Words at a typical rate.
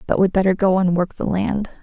No: fast, 265 wpm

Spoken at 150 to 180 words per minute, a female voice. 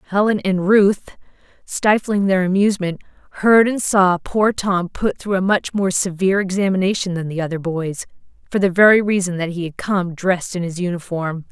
Yes: average, 175 wpm; female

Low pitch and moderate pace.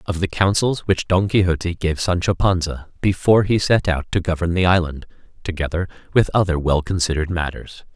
Yes: very low, 90 Hz; average, 175 wpm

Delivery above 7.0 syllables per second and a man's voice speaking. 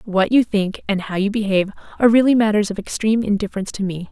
No: 7.2 syllables/s; female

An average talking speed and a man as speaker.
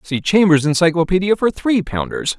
Yes: average, 150 wpm; male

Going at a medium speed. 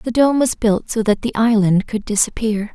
No: fast, 220 wpm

